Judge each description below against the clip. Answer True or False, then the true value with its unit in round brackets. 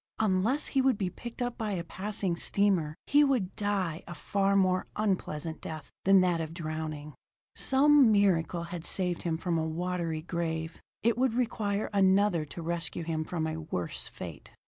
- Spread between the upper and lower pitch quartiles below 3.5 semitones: False (4.0 semitones)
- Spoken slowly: False (170 wpm)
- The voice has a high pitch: False (180 Hz)